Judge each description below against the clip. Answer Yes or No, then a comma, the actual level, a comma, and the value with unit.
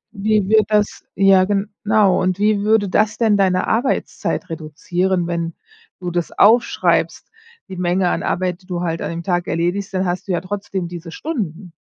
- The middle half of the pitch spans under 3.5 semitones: Yes, average, 2.8 semitones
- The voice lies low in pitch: No, medium, 185 Hz